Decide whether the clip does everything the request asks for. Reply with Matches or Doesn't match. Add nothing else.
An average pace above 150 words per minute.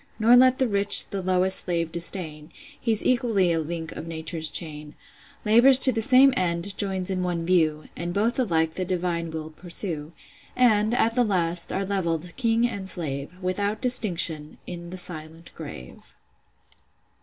Matches